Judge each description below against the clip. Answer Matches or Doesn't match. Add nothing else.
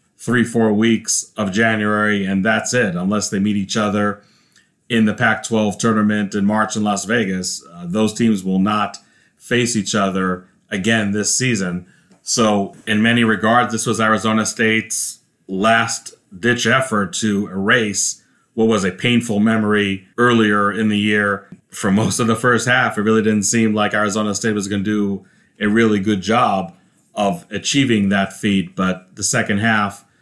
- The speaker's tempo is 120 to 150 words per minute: Doesn't match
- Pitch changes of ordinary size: Doesn't match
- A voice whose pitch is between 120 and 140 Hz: Doesn't match